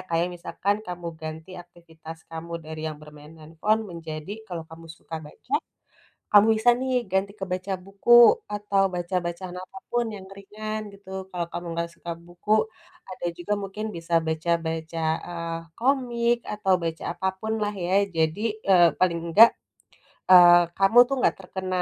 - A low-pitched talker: No, medium, 175 Hz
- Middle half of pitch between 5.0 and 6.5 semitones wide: No, average, 3.3 semitones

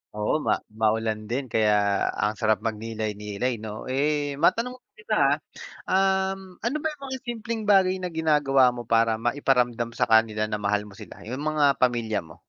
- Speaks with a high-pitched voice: No, low, 125 Hz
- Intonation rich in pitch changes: Yes, wide, 6.9 semitones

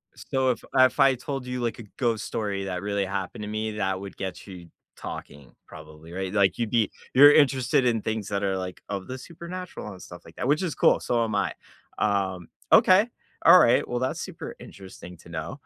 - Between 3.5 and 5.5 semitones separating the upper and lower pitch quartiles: Yes, average, 5.2 semitones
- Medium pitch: No, low, 105 Hz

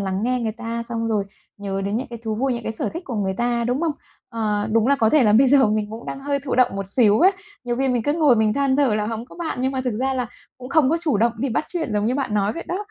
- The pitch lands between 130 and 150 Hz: No, high, 240 Hz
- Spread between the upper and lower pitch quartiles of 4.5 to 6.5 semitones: No, average, 3.8 semitones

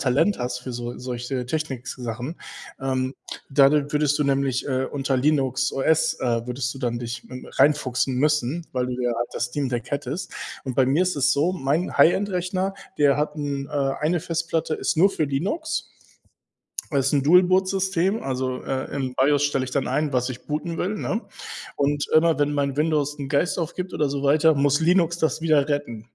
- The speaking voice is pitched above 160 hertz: No, medium, 140 Hz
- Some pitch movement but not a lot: Yes, average, 3.4 semitones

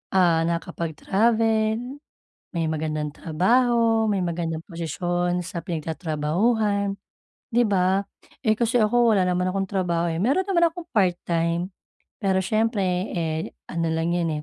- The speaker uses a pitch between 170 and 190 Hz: Yes, medium, 185 Hz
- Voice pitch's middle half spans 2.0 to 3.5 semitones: No, average, 4.8 semitones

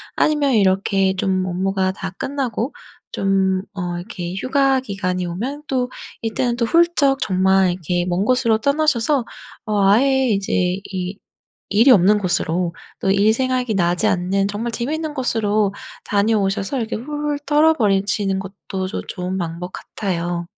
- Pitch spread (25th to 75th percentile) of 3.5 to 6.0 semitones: Yes, average, 5.2 semitones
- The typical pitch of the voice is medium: No, high, 200 Hz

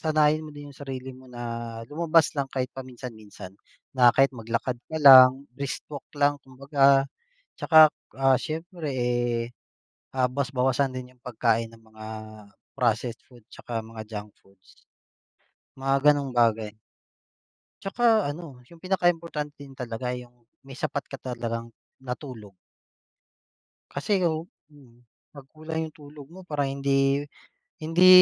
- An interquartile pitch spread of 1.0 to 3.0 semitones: No, average, 3.5 semitones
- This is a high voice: No, low, 135 Hz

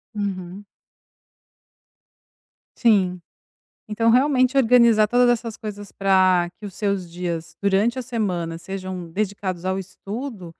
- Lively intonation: No, average, 3.8 semitones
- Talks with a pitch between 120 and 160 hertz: No, high, 200 Hz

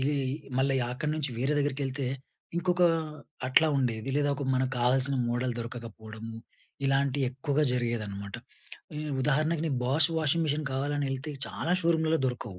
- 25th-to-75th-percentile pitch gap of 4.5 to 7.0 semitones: No, average, 3.3 semitones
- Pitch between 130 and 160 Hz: Yes, low, 135 Hz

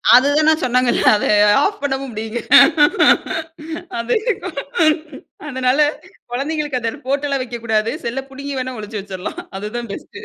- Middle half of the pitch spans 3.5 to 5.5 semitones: Yes, average, 3.8 semitones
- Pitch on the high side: Yes, very high, 255 Hz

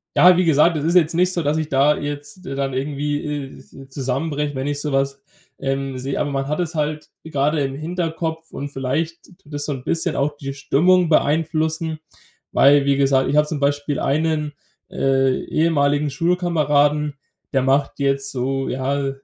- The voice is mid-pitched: Yes, medium, 145 Hz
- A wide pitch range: No, narrow, 2.6 semitones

